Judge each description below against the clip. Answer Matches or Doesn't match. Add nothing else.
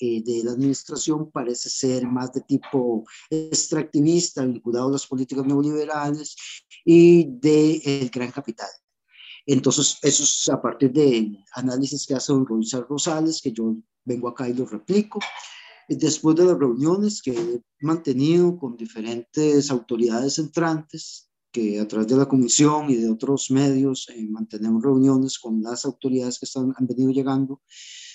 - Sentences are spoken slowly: Doesn't match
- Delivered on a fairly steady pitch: Doesn't match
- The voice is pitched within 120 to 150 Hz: Matches